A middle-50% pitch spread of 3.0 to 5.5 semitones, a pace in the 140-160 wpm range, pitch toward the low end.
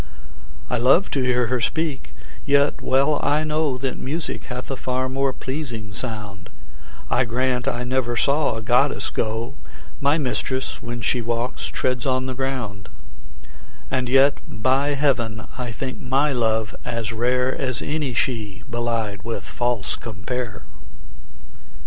No: narrow, 2.6 semitones; average, 145 wpm; low, 125 Hz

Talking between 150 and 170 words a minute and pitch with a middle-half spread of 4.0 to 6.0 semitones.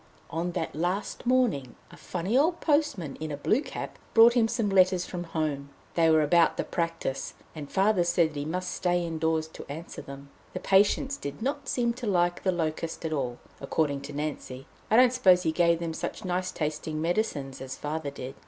No: average, 200 wpm; average, 4.4 semitones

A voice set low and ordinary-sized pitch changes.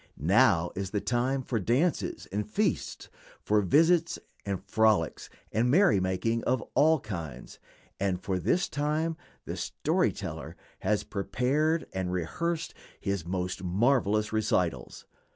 No: low, 105 Hz; wide, 6.3 semitones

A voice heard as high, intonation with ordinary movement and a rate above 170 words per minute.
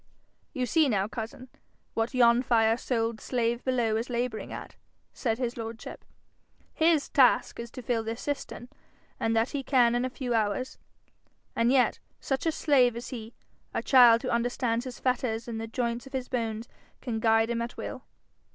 No: high, 240 Hz; narrow, 2.0 semitones; average, 180 wpm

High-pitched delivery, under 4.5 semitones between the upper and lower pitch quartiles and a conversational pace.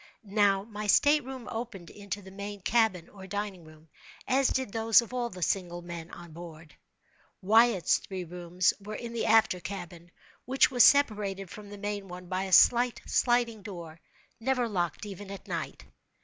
Yes: high, 200 Hz; average, 4.1 semitones; average, 175 wpm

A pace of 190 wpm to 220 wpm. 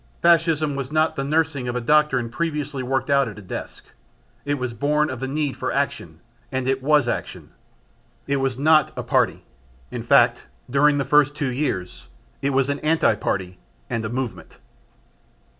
No: average, 175 wpm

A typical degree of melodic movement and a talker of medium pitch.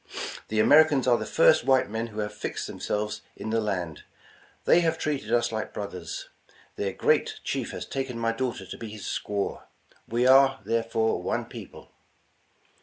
No: average, 3.6 semitones; low, 115 Hz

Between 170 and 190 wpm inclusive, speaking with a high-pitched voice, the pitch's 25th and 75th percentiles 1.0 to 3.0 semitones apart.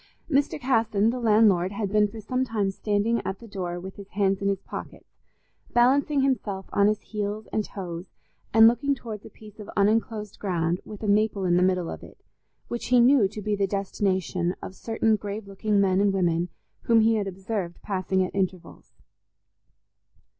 Yes: average, 185 wpm; high, 205 Hz; average, 2.7 semitones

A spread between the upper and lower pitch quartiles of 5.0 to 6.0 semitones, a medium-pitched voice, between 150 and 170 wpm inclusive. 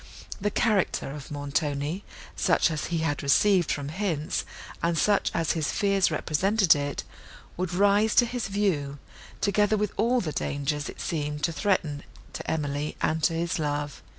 Yes: wide, 5.4 semitones; medium, 165 Hz; average, 160 wpm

